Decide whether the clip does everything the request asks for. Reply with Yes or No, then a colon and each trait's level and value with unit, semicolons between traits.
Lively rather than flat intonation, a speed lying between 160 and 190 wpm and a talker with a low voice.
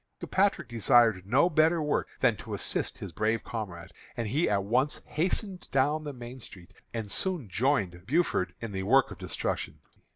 Yes: wide, 6.7 semitones; average, 170 wpm; low, 120 Hz